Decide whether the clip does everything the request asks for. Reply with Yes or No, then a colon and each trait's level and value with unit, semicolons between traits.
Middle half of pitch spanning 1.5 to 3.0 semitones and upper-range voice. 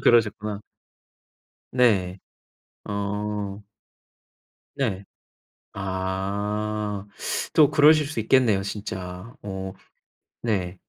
No: narrow, 2.4 semitones; low, 105 Hz